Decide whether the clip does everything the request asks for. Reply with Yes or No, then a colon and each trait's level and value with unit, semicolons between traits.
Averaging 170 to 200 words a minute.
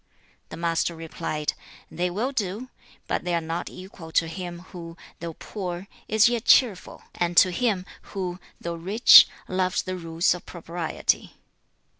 No: average, 150 wpm